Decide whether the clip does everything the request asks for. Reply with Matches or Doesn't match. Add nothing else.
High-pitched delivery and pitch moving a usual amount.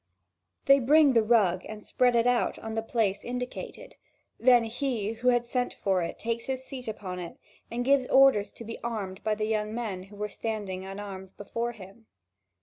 Matches